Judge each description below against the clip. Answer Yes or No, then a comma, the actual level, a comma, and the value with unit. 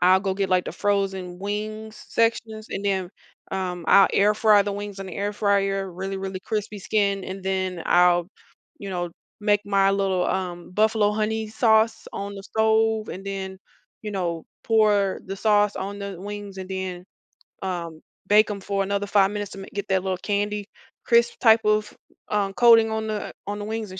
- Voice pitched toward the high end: Yes, high, 200 Hz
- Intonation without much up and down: Yes, narrow, 1.8 semitones